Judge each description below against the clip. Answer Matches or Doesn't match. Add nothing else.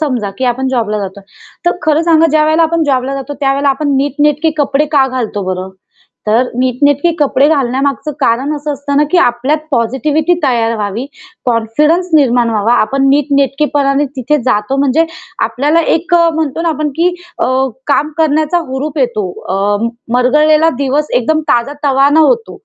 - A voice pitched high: Matches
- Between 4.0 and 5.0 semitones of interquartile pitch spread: Doesn't match